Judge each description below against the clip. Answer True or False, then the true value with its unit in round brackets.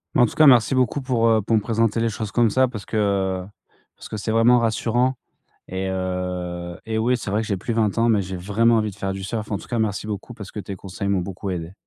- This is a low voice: True (105 Hz)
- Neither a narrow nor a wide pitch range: True (3.2 semitones)